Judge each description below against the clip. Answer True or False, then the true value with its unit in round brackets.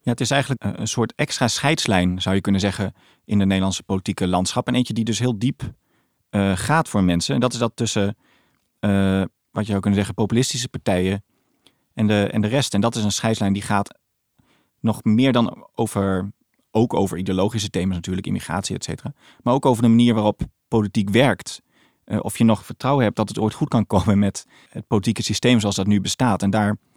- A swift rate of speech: True (210 wpm)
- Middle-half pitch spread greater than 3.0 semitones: True (3.4 semitones)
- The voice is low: True (105 Hz)